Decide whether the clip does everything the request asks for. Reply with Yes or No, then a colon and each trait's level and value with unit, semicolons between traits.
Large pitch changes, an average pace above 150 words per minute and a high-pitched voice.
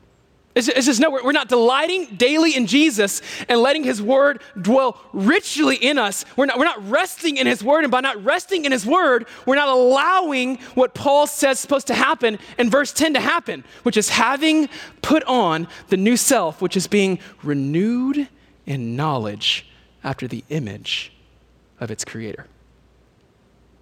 Yes: wide, 7.0 semitones; average, 170 wpm; very high, 255 Hz